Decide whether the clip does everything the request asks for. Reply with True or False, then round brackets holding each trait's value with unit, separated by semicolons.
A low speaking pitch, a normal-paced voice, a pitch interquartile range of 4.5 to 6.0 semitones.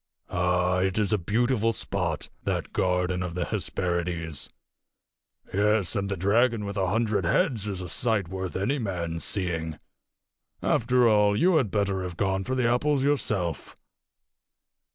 False (100 Hz; 150 wpm; 3.9 semitones)